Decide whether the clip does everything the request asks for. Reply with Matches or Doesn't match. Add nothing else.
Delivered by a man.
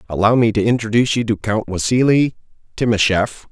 Matches